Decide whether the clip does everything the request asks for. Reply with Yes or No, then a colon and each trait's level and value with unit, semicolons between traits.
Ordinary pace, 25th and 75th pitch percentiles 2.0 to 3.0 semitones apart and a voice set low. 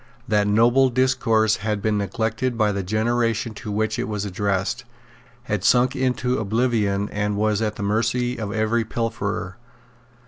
Yes: average, 150 wpm; narrow, 2.5 semitones; low, 110 Hz